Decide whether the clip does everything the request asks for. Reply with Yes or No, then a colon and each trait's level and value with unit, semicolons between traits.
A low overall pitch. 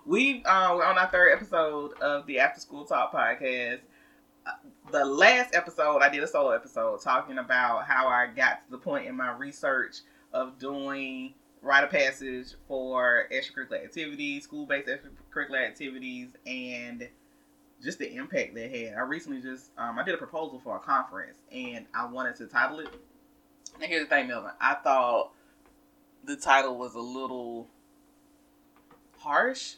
No: medium, 170 Hz